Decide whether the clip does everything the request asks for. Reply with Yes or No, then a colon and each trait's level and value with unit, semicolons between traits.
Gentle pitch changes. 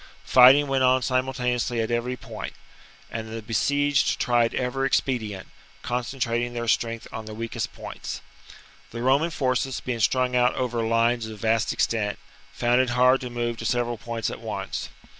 Yes: narrow, 1.8 semitones